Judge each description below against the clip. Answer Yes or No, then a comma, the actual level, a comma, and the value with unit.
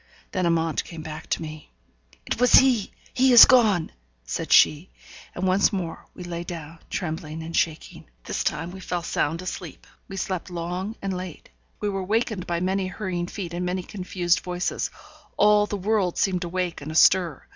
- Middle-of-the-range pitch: Yes, medium, 180 Hz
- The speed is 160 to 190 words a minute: Yes, average, 180 wpm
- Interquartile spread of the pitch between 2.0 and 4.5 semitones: Yes, narrow, 2.6 semitones